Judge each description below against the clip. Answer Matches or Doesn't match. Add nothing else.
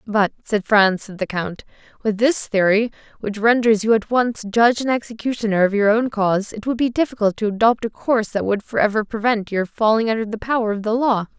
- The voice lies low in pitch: Doesn't match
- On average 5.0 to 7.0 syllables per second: Matches